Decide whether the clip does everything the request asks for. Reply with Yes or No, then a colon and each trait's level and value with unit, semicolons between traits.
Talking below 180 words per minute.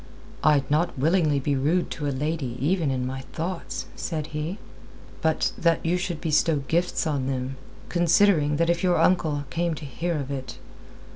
Yes: average, 170 wpm